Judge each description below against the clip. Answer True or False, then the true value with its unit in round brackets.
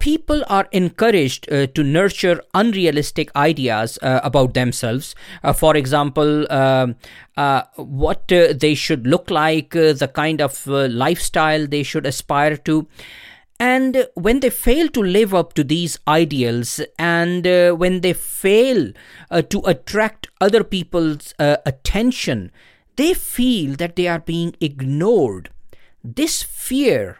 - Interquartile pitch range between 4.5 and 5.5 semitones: True (4.9 semitones)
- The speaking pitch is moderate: True (160 Hz)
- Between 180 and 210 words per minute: False (140 wpm)